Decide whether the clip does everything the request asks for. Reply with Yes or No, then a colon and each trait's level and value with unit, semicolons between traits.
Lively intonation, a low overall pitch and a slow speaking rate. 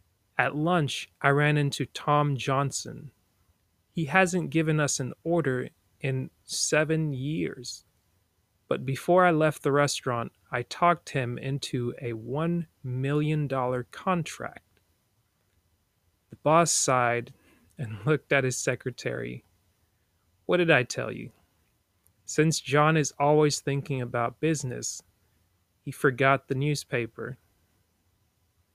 Yes: wide, 6.8 semitones; low, 130 Hz; slow, 115 wpm